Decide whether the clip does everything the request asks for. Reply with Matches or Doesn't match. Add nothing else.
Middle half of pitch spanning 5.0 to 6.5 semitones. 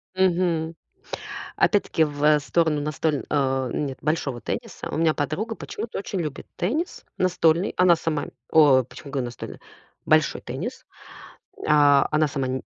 Doesn't match